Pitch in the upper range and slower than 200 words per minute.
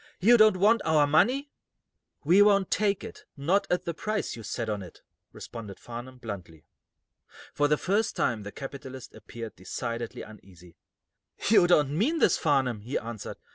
No: medium, 140 Hz; average, 160 wpm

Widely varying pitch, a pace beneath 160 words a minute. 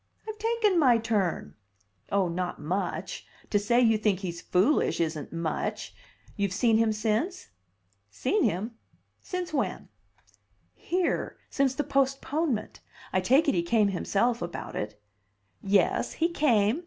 Yes: wide, 6.9 semitones; slow, 135 wpm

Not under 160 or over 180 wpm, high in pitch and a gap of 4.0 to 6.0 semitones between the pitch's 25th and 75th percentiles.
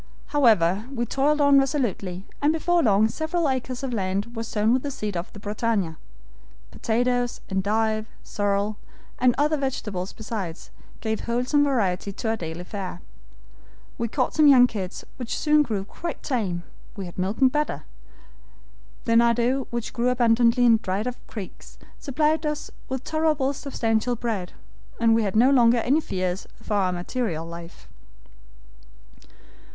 No: average, 150 wpm; high, 230 Hz; average, 4.7 semitones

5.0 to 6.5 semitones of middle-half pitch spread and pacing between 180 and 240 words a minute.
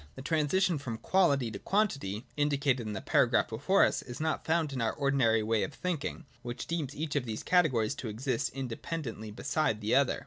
Yes: wide, 5.4 semitones; fast, 205 wpm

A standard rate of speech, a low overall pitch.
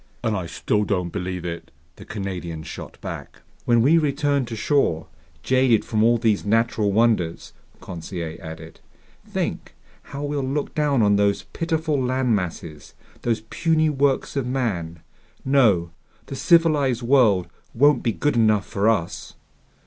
Yes: average, 145 wpm; low, 115 Hz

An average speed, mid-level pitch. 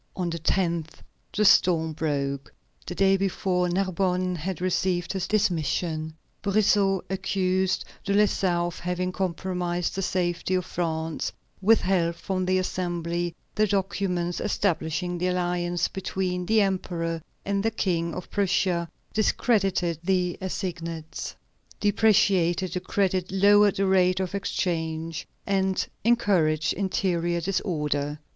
No: slow, 120 wpm; medium, 180 Hz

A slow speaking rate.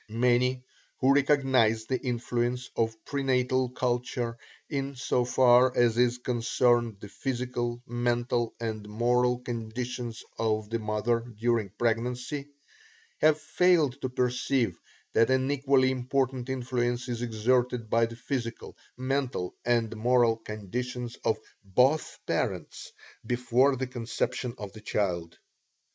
Yes: slow, 125 wpm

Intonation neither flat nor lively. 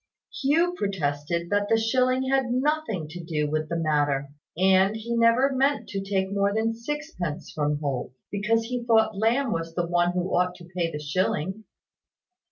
No: wide, 5.9 semitones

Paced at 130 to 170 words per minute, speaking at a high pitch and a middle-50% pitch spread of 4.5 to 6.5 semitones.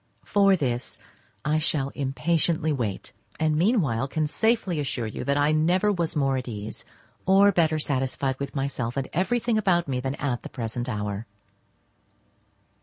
No: average, 155 wpm; medium, 145 Hz; average, 5.0 semitones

